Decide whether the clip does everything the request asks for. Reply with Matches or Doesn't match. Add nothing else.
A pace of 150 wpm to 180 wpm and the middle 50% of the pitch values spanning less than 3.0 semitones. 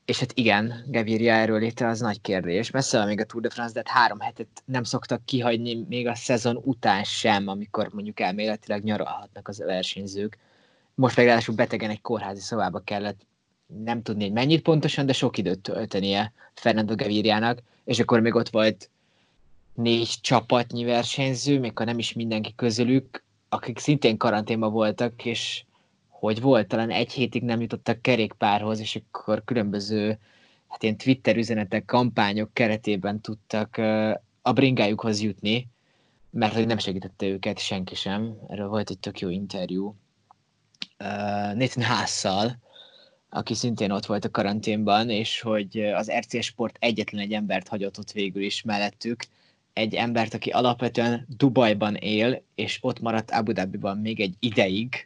Matches